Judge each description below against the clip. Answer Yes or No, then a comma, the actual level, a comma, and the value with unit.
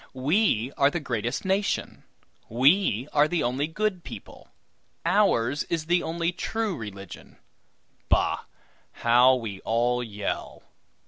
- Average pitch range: No, wide, 6.9 semitones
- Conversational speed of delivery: No, slow, 120 wpm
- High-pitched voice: No, medium, 140 Hz